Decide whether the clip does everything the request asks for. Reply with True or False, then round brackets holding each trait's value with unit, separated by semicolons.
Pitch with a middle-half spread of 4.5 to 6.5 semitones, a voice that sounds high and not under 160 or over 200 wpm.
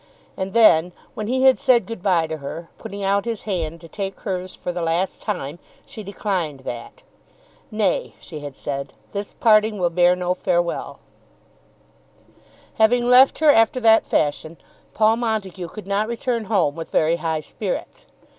True (4.8 semitones; 195 Hz; 165 wpm)